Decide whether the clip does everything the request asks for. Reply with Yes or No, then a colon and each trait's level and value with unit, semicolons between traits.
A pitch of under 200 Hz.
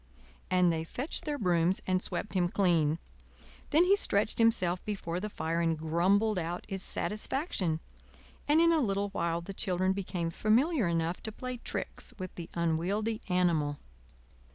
Yes: medium, 185 Hz